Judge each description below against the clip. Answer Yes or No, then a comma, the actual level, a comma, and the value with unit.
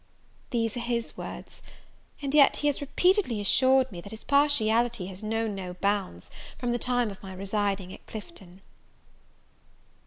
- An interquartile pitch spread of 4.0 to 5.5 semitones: Yes, average, 4.6 semitones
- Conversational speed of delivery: Yes, average, 155 wpm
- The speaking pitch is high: Yes, high, 225 Hz